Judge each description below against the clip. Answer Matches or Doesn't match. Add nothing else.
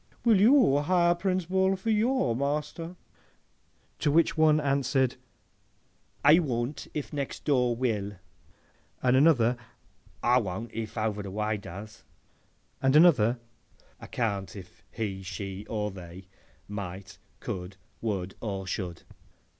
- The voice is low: Matches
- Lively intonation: Matches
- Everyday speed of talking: Doesn't match